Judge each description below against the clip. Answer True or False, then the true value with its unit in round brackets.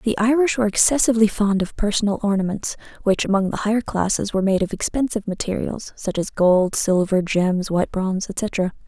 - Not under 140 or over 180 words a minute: True (175 wpm)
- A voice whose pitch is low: False (205 Hz)